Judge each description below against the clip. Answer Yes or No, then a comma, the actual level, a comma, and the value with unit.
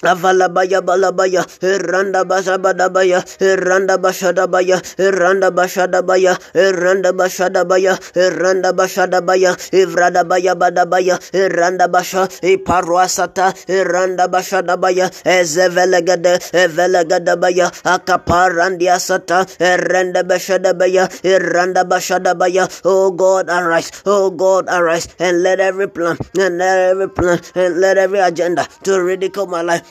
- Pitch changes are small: Yes, narrow, 0.8 semitones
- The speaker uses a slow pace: Yes, slow, 130 wpm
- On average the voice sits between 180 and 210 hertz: Yes, medium, 185 Hz